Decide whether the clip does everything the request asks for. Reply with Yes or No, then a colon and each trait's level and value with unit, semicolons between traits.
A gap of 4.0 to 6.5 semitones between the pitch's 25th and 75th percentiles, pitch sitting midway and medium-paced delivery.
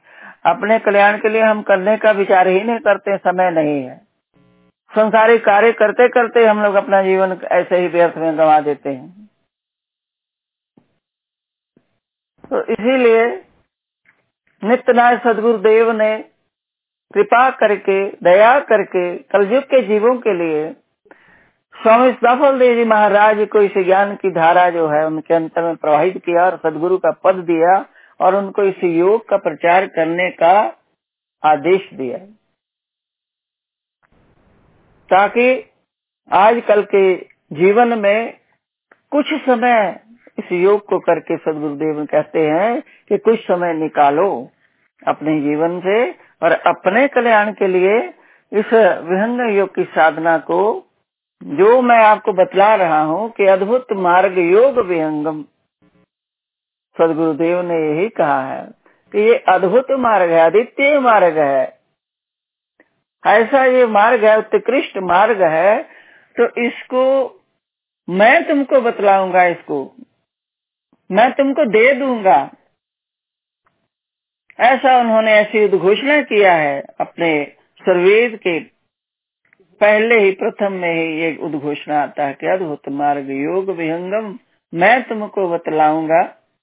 No: wide, 5.4 semitones; high, 200 Hz; average, 125 wpm